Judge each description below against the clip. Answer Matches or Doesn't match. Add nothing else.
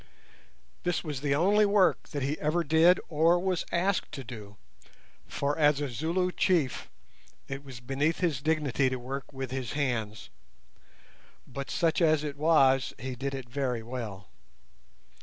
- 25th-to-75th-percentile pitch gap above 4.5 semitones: Doesn't match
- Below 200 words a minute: Matches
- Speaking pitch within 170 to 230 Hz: Doesn't match